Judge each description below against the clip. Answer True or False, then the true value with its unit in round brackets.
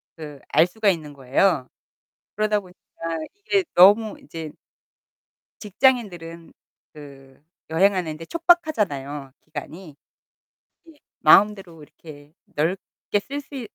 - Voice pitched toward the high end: False (175 Hz)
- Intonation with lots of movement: True (5.8 semitones)